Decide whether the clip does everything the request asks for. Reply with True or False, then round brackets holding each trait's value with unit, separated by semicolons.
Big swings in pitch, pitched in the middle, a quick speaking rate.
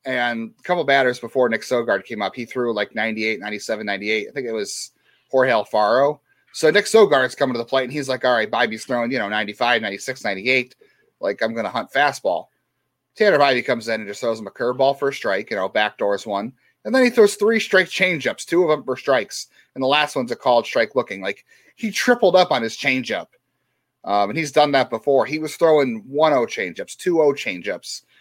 False (6.6 semitones; 130 Hz; 230 wpm)